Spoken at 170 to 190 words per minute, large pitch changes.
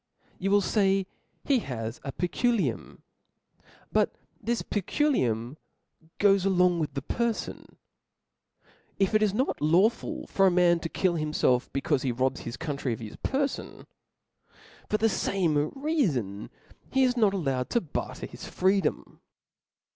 No: average, 145 wpm; wide, 7.6 semitones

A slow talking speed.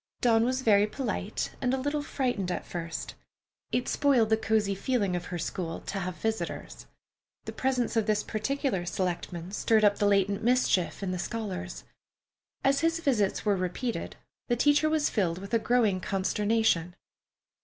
No: average, 165 wpm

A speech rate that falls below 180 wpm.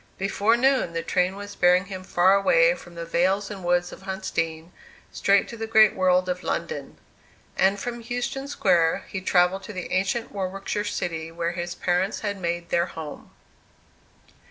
Yes: average, 170 wpm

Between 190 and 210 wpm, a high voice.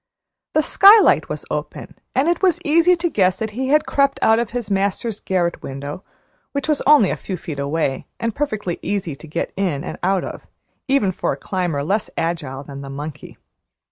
Yes: average, 195 wpm; high, 195 Hz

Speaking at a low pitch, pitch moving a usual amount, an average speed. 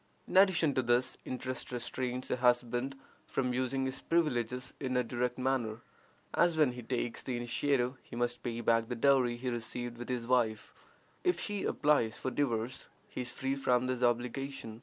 No: low, 125 Hz; narrow, 1.8 semitones; average, 180 wpm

